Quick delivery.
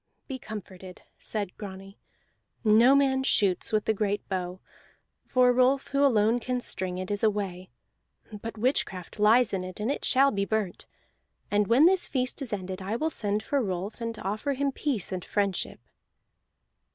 No: average, 165 wpm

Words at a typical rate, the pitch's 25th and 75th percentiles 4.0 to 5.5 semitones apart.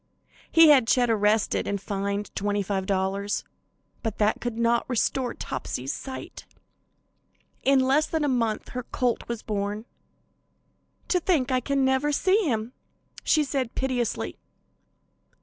No: slow, 130 wpm; average, 4.4 semitones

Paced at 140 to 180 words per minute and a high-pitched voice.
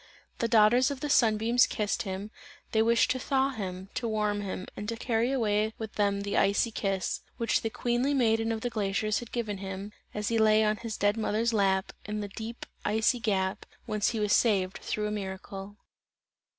No: average, 200 wpm; high, 215 Hz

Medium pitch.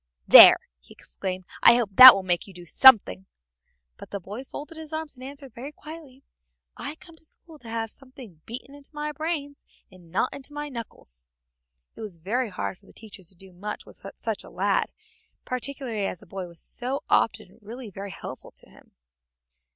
No: high, 235 Hz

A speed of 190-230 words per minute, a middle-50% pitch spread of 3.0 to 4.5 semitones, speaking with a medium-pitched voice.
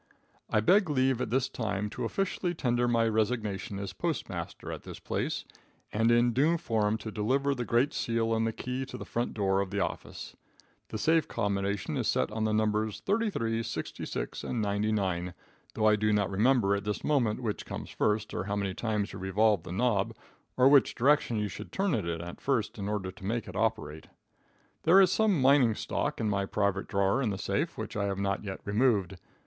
No: average, 200 wpm; average, 3.7 semitones; low, 110 Hz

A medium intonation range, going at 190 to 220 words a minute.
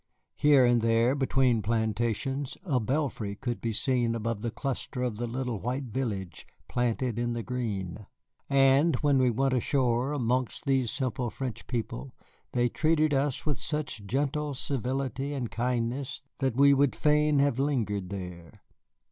No: average, 3.0 semitones; average, 150 wpm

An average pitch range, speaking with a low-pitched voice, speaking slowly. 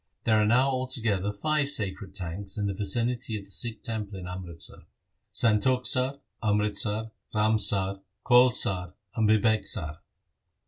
Yes: average, 3.2 semitones; low, 105 Hz; slow, 130 wpm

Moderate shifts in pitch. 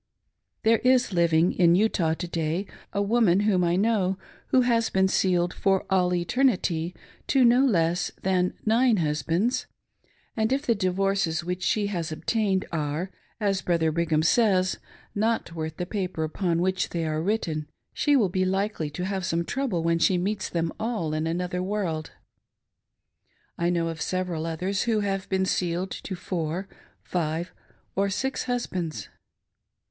Yes: average, 3.5 semitones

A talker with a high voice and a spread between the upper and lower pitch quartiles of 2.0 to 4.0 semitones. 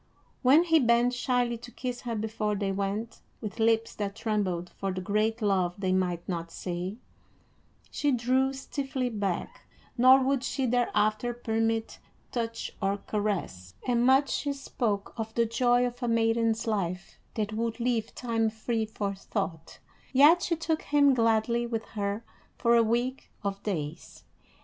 Yes: high, 225 Hz; average, 3.3 semitones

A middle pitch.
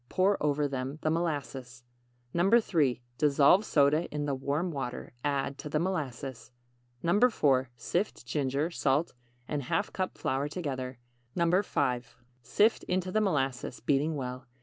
Yes: medium, 145 Hz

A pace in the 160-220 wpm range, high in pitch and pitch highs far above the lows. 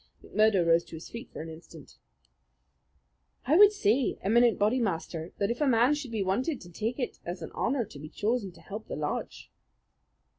Yes: average, 195 wpm; high, 215 Hz; wide, 5.8 semitones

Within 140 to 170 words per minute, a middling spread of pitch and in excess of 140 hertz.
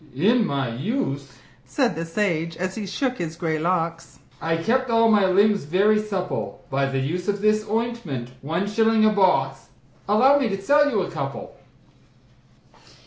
Yes: average, 165 wpm; average, 5.0 semitones; high, 190 Hz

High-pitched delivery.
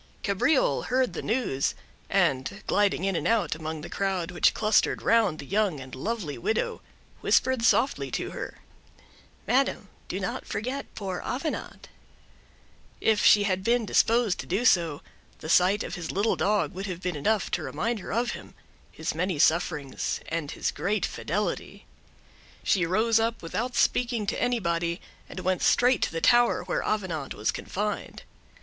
Yes: high, 200 Hz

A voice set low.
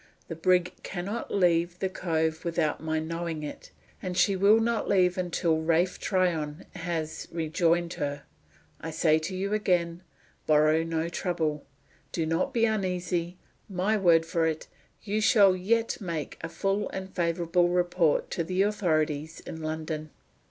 No: medium, 170 Hz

